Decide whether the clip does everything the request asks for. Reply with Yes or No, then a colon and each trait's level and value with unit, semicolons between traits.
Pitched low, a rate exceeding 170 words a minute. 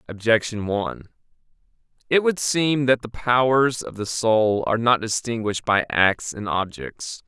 No: low, 115 Hz; average, 150 wpm